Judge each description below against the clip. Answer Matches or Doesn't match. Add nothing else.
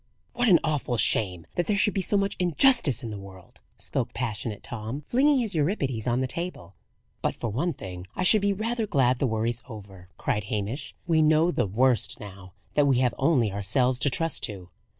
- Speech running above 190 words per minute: Matches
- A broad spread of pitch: Matches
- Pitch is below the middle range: Matches